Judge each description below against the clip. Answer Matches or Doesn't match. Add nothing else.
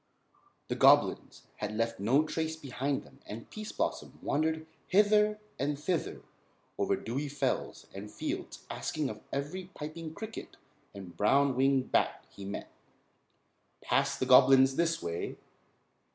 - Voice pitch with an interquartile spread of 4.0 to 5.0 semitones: Matches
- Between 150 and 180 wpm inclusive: Doesn't match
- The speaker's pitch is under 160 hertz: Matches